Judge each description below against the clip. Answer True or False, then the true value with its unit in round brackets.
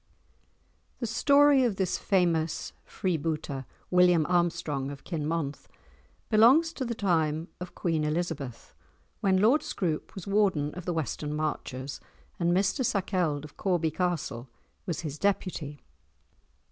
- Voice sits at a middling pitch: True (170 Hz)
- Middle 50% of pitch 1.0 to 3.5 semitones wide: False (4.2 semitones)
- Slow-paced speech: True (125 wpm)